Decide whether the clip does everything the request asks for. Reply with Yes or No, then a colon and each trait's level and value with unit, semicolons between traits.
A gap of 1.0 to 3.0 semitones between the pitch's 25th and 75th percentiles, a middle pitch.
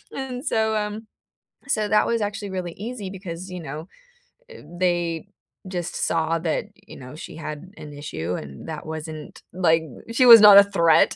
No: average, 4.7 semitones; medium, 180 Hz